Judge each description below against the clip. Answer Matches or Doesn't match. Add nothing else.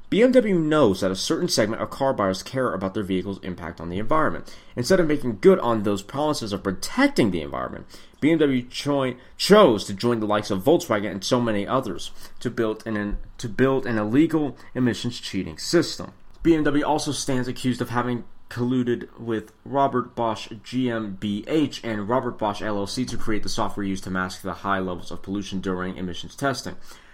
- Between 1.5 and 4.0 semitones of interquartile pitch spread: Doesn't match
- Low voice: Matches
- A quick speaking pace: Doesn't match